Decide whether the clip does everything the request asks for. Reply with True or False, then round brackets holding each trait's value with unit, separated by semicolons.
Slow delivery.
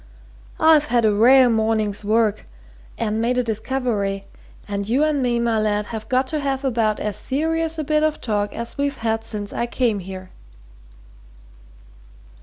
False (165 wpm)